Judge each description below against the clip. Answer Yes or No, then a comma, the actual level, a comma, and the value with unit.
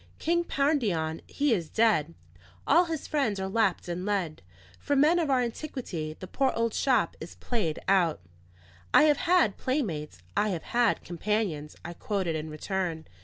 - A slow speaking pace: No, average, 165 wpm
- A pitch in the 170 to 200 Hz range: No, high, 210 Hz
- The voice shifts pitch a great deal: Yes, wide, 8.4 semitones